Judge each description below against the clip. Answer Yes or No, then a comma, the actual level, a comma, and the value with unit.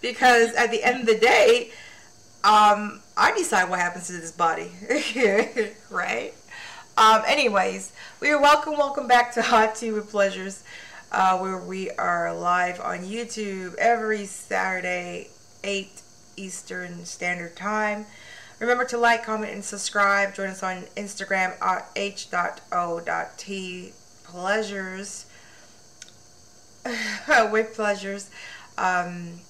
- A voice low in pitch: No, high, 200 Hz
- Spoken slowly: Yes, slow, 115 wpm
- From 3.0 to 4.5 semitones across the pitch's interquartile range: Yes, average, 3.3 semitones